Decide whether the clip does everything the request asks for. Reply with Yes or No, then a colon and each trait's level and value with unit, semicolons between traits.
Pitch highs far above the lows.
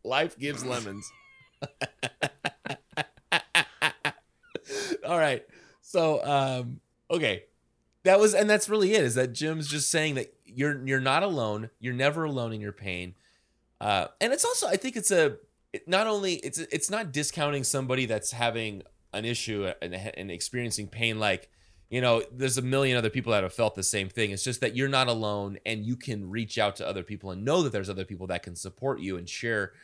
Yes: wide, 6.1 semitones